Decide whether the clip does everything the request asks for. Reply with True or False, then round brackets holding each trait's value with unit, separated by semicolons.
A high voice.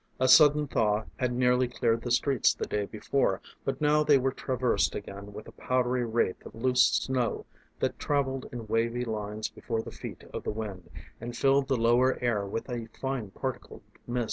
False (120 Hz)